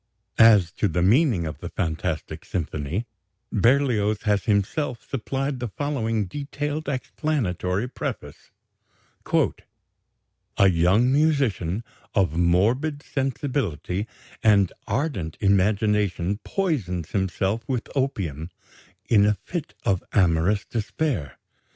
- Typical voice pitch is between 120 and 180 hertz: No, low, 105 Hz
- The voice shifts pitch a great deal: Yes, wide, 6.7 semitones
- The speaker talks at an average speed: No, slow, 100 wpm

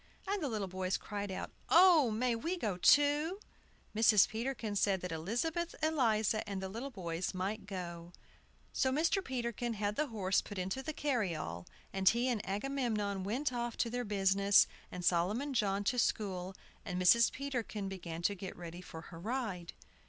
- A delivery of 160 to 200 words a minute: Yes, average, 170 wpm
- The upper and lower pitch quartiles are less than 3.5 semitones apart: No, average, 5.1 semitones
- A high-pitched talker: Yes, high, 210 Hz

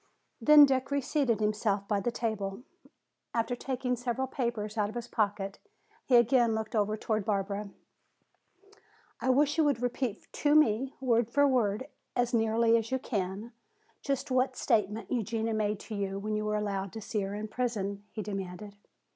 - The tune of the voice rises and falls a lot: No, average, 3.3 semitones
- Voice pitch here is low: No, high, 225 Hz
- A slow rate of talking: No, average, 170 wpm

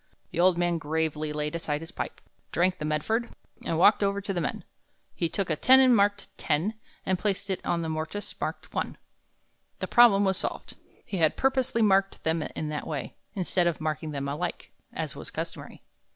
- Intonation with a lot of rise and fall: No, average, 4.3 semitones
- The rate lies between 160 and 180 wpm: No, average, 190 wpm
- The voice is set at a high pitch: No, medium, 175 Hz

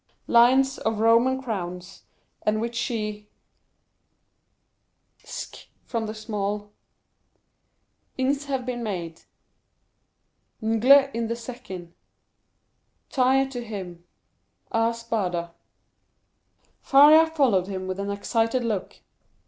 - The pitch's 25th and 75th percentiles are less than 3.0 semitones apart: No, average, 4.0 semitones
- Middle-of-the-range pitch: No, high, 225 Hz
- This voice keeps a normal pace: No, slow, 100 wpm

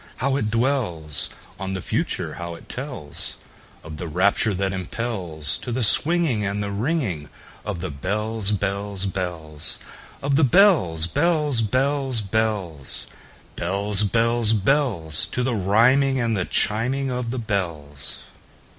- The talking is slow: Yes, slow, 115 wpm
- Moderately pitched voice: No, low, 105 Hz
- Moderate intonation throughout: No, wide, 5.7 semitones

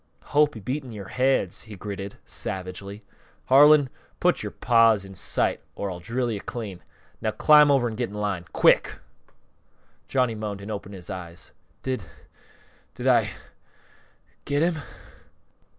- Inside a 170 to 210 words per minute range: No, average, 150 wpm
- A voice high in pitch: No, low, 110 Hz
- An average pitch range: Yes, average, 4.8 semitones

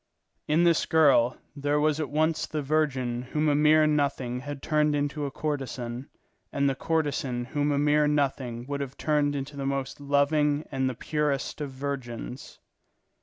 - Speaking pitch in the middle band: Yes, medium, 145 Hz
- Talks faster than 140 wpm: Yes, average, 170 wpm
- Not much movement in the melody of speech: Yes, narrow, 2.0 semitones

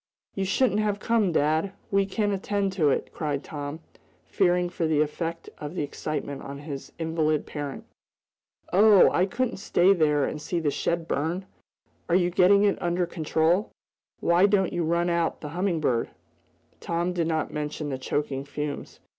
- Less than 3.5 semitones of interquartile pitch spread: No, average, 4.0 semitones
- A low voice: No, medium, 170 Hz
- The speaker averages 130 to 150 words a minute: No, average, 170 wpm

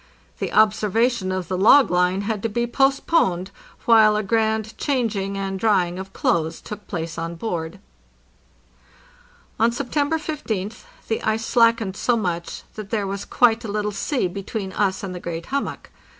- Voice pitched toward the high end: Yes, high, 210 Hz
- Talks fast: No, average, 165 wpm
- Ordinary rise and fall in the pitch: Yes, average, 3.5 semitones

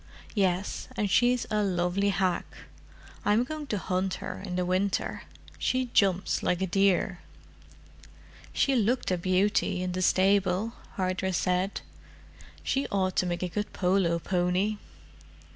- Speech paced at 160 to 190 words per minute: No, slow, 135 wpm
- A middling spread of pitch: No, narrow, 2.3 semitones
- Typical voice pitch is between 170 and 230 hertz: Yes, high, 190 Hz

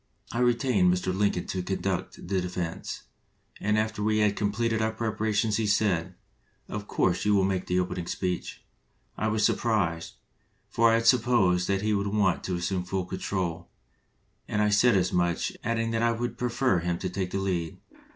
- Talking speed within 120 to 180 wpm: No, average, 190 wpm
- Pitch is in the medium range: No, low, 100 Hz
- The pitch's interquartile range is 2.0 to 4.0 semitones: Yes, average, 3.3 semitones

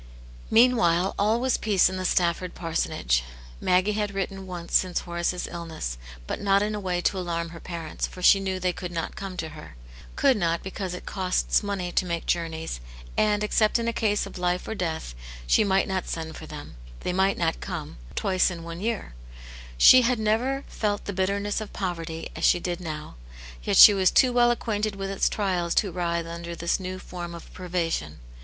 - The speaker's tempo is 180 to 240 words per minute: Yes, average, 200 wpm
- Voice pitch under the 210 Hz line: Yes, medium, 185 Hz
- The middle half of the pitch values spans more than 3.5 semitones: No, average, 3.1 semitones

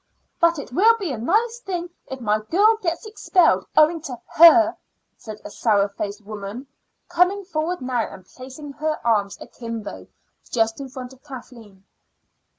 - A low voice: No, very high, 270 Hz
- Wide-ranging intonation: Yes, wide, 7.5 semitones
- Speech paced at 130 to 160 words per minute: Yes, average, 155 wpm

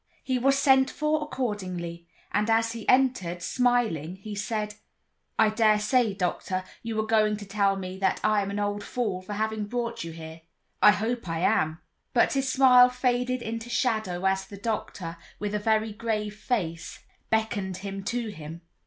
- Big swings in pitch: No, average, 3.7 semitones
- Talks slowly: No, average, 175 wpm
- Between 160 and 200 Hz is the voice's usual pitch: No, high, 210 Hz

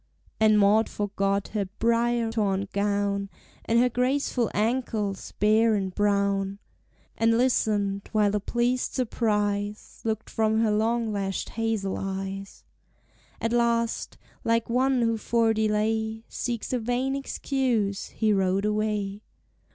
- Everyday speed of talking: No, slow, 125 wpm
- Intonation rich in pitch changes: No, narrow, 2.4 semitones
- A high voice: Yes, high, 220 Hz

